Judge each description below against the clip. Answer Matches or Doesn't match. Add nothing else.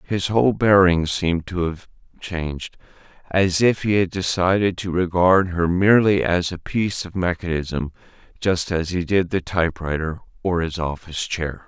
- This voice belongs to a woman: Doesn't match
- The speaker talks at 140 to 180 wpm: Matches